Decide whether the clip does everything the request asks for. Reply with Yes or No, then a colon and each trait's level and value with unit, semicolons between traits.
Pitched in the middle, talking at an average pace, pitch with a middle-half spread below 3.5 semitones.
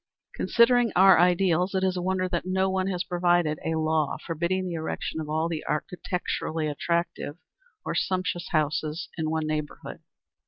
Yes: medium, 175 Hz; average, 160 wpm; average, 2.8 semitones